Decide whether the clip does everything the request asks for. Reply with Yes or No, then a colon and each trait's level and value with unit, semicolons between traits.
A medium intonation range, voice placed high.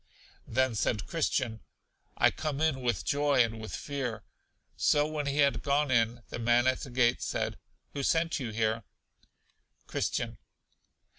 No: average, 3.7 semitones; low, 130 Hz